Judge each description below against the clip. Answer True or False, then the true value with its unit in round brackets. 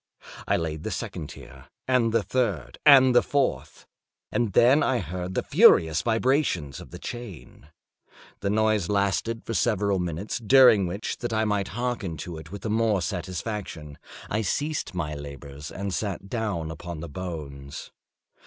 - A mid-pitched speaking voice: False (100 Hz)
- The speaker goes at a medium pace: True (160 wpm)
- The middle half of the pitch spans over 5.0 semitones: True (5.6 semitones)